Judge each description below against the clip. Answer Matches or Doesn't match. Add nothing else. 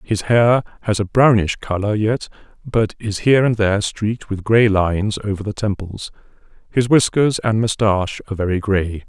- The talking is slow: Doesn't match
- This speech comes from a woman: Doesn't match